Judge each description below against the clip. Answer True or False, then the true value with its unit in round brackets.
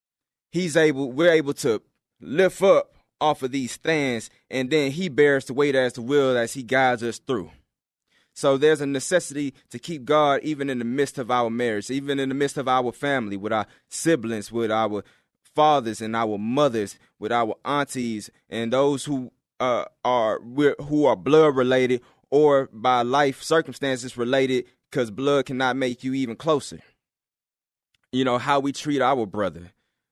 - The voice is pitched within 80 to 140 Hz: True (135 Hz)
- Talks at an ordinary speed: True (170 wpm)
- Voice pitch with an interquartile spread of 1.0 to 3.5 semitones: True (3.1 semitones)